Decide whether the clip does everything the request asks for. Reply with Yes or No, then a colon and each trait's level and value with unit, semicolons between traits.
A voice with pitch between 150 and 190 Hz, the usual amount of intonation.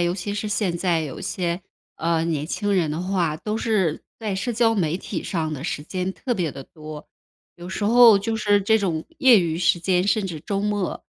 Yes: medium, 185 Hz; average, 3.9 semitones